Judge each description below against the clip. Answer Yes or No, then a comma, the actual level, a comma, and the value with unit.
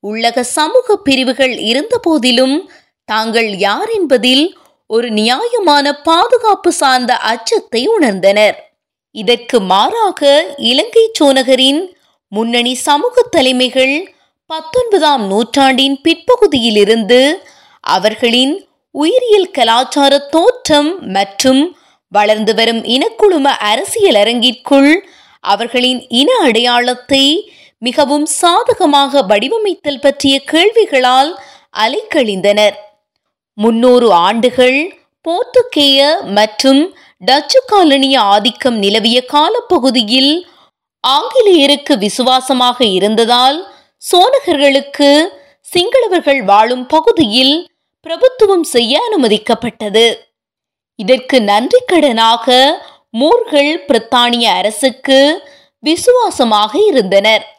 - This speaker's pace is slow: Yes, slow, 65 wpm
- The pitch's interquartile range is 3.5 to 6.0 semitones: Yes, wide, 5.4 semitones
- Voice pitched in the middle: No, very high, 275 Hz